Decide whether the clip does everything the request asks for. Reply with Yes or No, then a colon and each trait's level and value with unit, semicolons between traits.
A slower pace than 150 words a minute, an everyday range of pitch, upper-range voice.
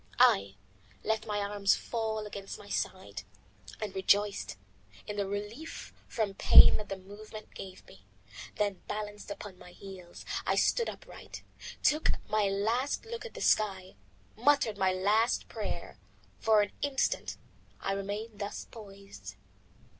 No: average, 140 wpm; narrow, 1.9 semitones; high, 205 Hz